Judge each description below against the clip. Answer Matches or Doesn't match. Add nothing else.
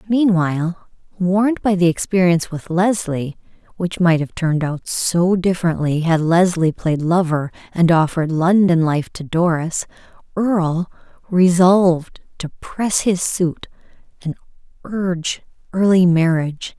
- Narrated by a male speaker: Doesn't match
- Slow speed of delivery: Matches